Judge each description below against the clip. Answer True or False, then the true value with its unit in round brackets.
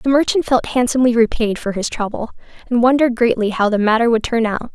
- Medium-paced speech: False (215 wpm)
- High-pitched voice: True (235 Hz)